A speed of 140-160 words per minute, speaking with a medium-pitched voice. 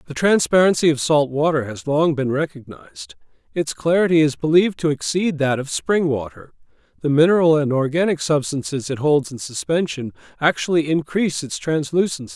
Yes: average, 155 wpm; medium, 155 Hz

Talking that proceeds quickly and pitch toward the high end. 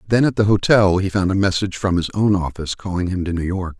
No: fast, 270 wpm; very low, 95 Hz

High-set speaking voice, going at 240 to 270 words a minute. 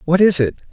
No: medium, 165 Hz; fast, 250 wpm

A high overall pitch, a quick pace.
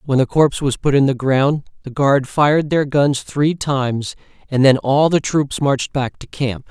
No: medium, 140 Hz; fast, 215 wpm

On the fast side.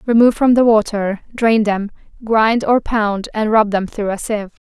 No: average, 195 wpm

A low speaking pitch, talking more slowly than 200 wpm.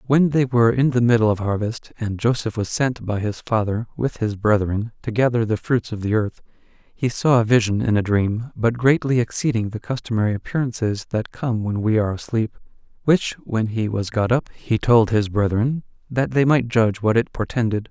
No: low, 115 Hz; fast, 205 wpm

